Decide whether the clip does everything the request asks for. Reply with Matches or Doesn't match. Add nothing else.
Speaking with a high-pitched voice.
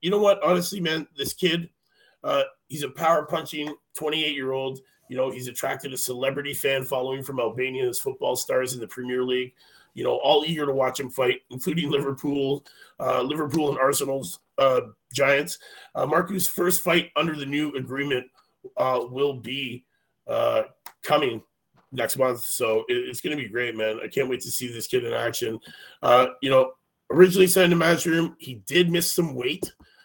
Doesn't match